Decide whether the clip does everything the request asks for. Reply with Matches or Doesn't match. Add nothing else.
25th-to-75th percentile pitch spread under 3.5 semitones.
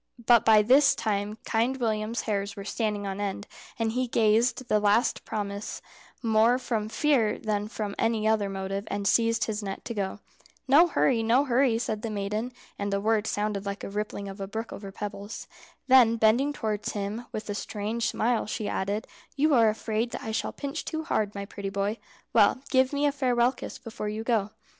Matches